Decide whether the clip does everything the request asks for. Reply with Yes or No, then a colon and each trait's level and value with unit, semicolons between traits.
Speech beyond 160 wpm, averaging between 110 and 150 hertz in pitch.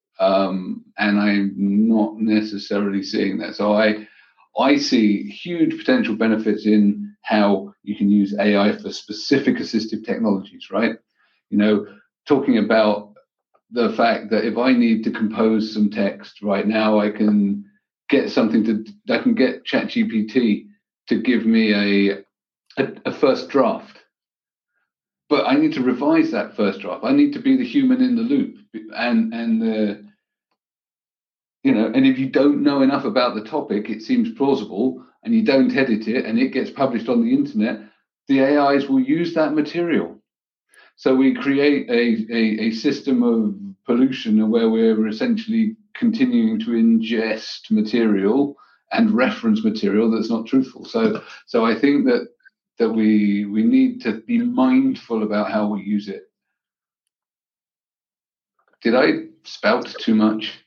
No: average, 155 wpm; medium, 140 Hz